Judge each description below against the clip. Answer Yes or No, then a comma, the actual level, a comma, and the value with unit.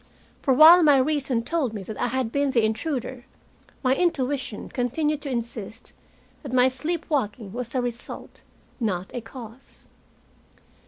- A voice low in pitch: No, very high, 255 Hz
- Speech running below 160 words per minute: Yes, average, 145 wpm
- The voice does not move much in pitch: No, average, 3.7 semitones